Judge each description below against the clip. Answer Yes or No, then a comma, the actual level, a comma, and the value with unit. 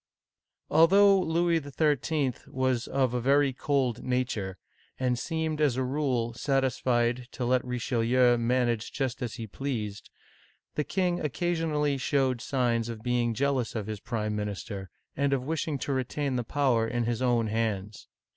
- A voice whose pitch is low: Yes, low, 125 Hz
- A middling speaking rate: Yes, average, 150 wpm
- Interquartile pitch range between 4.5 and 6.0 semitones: No, average, 3.3 semitones